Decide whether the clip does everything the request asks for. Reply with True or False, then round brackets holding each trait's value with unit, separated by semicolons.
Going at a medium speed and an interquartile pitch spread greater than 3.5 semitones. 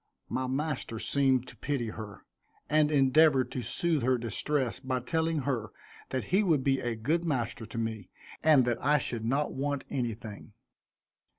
True (165 wpm; 4.0 semitones)